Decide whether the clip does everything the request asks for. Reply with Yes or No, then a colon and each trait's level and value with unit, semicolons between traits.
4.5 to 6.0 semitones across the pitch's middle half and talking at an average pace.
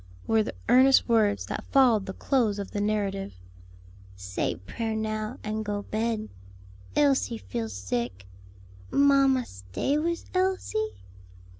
No: average, 5.2 semitones; slow, 125 wpm